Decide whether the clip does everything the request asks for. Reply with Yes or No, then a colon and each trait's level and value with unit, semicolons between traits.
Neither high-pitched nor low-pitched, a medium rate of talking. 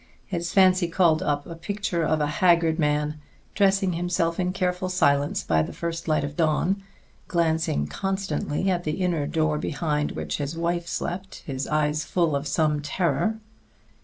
Yes: medium, 165 Hz; average, 160 wpm